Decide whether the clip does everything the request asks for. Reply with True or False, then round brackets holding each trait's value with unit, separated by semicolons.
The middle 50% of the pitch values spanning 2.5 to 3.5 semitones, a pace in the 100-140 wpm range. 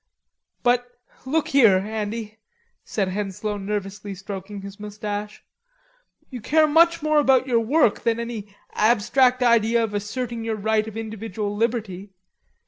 True (2.9 semitones; 135 wpm)